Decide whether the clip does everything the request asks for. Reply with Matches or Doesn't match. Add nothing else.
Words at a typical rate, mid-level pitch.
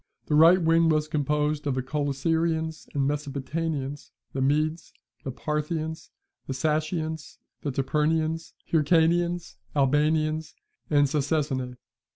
Doesn't match